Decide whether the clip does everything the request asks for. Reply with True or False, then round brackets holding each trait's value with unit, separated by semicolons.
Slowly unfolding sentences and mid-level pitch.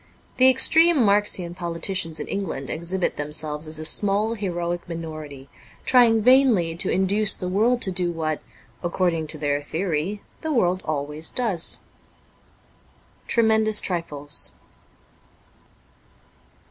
True (120 wpm; 180 Hz)